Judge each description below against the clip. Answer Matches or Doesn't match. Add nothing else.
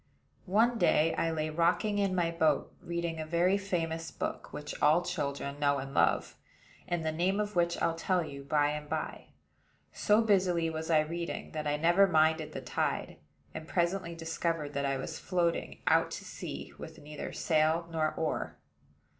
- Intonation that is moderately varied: Doesn't match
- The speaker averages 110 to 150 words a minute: Doesn't match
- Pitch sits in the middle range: Matches